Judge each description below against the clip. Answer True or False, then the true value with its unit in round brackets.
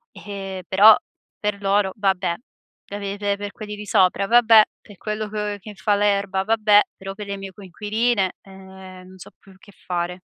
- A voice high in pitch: True (200 Hz)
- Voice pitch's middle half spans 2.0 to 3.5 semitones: False (1.6 semitones)